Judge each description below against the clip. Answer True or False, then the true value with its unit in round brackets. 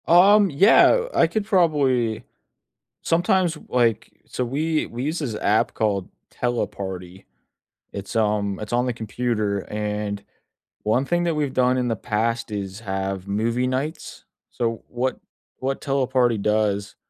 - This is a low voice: True (120 Hz)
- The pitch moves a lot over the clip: False (4.9 semitones)